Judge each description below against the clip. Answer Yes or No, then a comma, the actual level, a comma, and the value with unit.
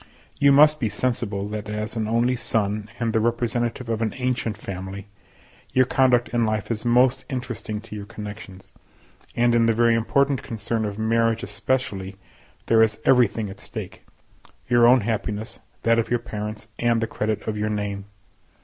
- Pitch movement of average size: No, narrow, 2.2 semitones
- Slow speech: No, average, 165 wpm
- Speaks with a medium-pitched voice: No, low, 115 Hz